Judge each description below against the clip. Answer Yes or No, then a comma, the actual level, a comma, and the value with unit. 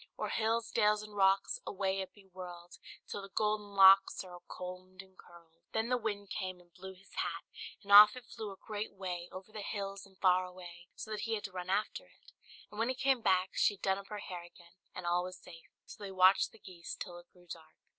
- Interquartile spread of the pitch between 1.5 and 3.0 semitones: Yes, narrow, 2.5 semitones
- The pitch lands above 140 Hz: Yes, high, 190 Hz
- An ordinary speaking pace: No, fast, 240 wpm